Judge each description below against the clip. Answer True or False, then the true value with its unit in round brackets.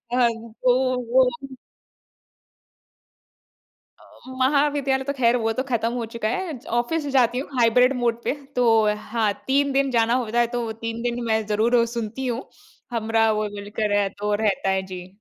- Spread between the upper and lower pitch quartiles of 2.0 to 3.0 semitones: True (2.7 semitones)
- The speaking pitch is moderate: False (235 Hz)